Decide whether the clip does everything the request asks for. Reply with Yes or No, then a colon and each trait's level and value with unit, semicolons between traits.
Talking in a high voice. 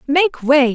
Yes: very high, 285 Hz